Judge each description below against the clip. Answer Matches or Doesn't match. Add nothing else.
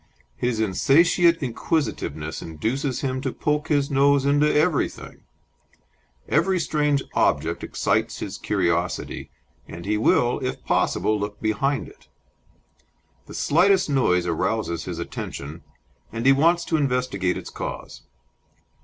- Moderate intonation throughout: Doesn't match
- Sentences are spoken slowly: Matches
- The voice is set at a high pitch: Doesn't match